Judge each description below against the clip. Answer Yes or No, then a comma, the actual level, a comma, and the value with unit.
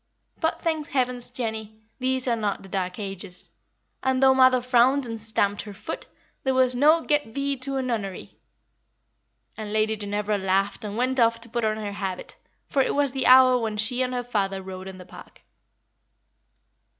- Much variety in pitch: No, average, 4.1 semitones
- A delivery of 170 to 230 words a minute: Yes, average, 185 wpm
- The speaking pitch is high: Yes, high, 230 Hz